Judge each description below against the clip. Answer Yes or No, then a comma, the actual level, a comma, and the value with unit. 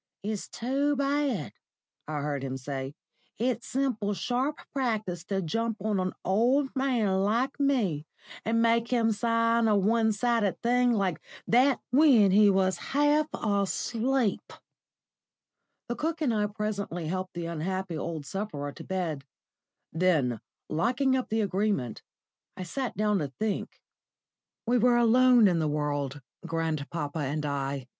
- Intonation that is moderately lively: No, wide, 6.4 semitones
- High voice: Yes, high, 210 Hz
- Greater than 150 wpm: No, average, 140 wpm